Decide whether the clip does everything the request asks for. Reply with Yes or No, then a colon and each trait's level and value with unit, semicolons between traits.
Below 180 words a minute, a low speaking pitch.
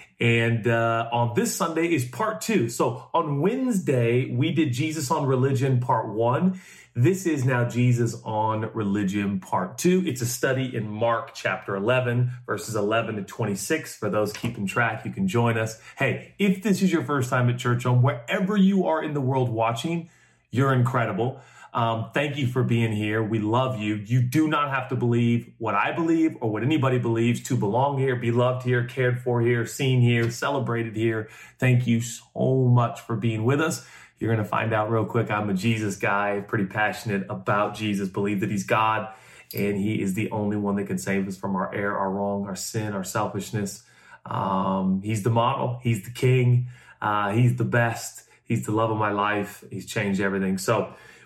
No: average, 195 wpm; low, 115 Hz